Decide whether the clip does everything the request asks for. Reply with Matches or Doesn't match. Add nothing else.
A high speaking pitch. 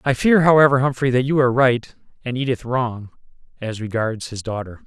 Doesn't match